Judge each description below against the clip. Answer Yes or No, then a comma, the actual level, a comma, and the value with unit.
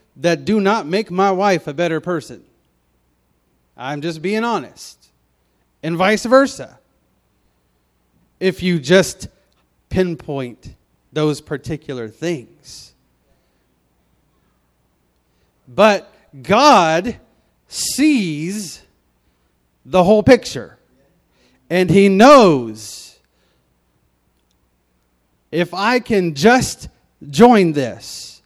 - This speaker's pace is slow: Yes, slow, 80 wpm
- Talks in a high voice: No, low, 135 Hz